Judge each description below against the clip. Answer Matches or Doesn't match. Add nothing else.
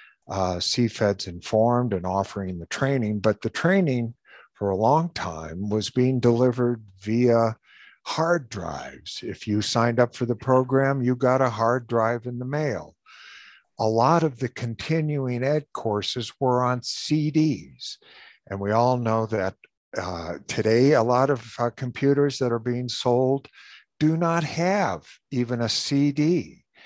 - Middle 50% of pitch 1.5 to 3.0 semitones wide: Doesn't match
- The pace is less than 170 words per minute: Matches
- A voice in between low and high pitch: Doesn't match